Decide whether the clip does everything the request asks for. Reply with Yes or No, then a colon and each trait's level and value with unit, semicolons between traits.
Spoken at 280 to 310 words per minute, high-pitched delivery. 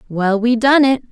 No: fast, 215 wpm; high, 235 Hz